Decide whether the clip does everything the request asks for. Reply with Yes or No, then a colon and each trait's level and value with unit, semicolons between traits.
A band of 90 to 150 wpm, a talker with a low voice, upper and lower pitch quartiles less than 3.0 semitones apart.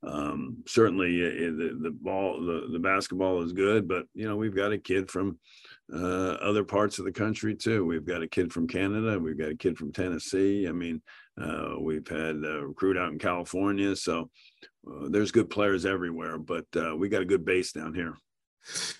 No: average, 200 wpm; very low, 95 Hz; narrow, 2.6 semitones